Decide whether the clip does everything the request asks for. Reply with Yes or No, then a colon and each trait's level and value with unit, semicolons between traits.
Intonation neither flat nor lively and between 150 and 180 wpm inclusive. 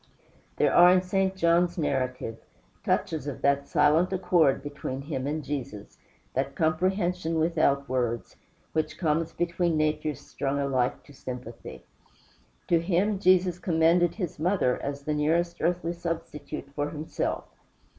No: average, 3.7 semitones; slow, 135 wpm